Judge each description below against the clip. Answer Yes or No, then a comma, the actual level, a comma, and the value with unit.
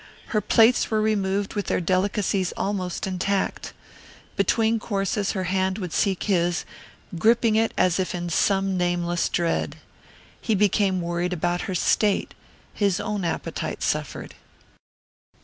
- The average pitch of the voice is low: No, high, 190 Hz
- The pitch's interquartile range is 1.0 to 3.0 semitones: Yes, narrow, 2.6 semitones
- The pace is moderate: No, slow, 130 wpm